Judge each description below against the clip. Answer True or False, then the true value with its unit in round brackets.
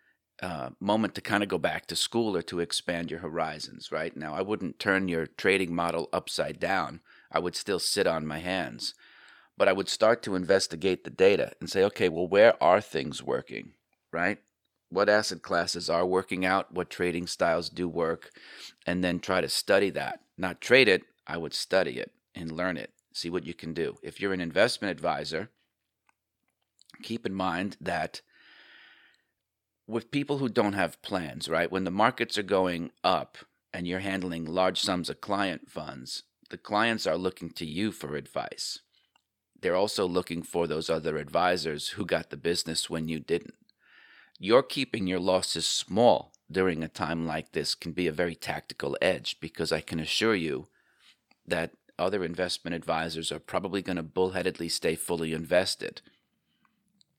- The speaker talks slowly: False (175 wpm)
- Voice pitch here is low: True (90 Hz)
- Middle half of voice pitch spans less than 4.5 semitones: True (2.9 semitones)